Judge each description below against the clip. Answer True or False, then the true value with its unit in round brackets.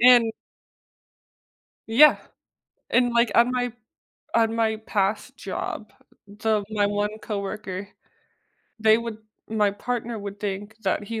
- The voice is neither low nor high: False (220 Hz)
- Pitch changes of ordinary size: False (2.2 semitones)